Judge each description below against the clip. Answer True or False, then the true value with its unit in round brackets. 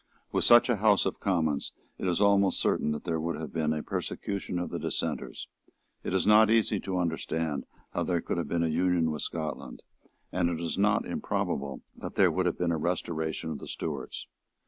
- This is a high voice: False (85 Hz)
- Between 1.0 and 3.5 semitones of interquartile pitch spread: True (3.2 semitones)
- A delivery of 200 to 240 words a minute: True (205 wpm)